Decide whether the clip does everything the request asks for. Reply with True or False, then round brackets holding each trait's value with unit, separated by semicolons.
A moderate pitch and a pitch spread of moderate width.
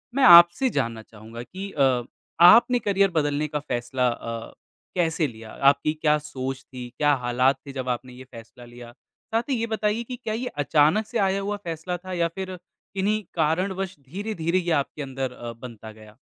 False (150 Hz; 7.5 semitones)